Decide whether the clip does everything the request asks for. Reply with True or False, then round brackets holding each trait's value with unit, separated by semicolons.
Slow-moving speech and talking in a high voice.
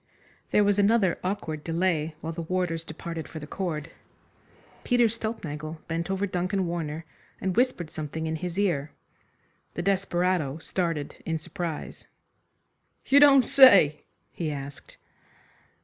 False (130 wpm; 170 Hz)